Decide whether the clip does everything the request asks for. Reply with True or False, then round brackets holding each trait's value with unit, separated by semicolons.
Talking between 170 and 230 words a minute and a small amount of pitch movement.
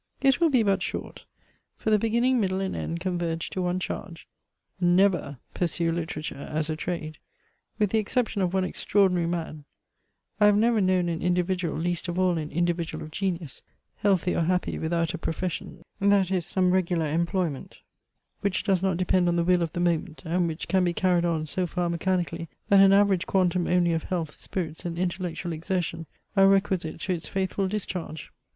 True (185 wpm; 2.2 semitones)